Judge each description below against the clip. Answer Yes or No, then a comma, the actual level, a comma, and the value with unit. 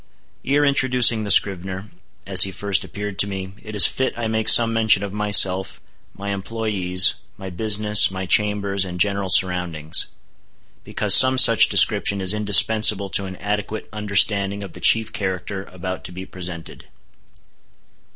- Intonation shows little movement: Yes, narrow, 2.3 semitones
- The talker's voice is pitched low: Yes, low, 100 Hz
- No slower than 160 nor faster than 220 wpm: No, average, 150 wpm